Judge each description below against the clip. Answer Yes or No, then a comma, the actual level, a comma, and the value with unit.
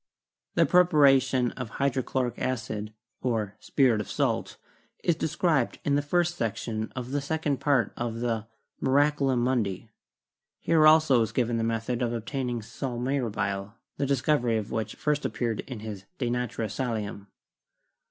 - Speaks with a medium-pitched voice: No, low, 125 Hz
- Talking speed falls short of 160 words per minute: Yes, average, 150 wpm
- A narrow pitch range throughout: No, average, 3.7 semitones